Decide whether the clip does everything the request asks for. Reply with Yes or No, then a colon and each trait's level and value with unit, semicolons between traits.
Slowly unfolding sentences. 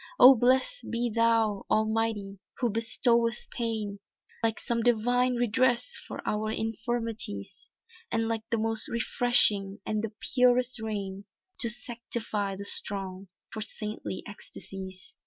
Yes: slow, 120 wpm